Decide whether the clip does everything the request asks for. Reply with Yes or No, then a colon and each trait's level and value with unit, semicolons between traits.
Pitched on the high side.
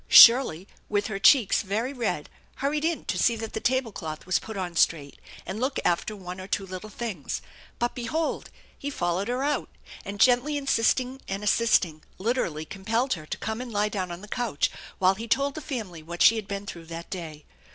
Yes: high, 210 Hz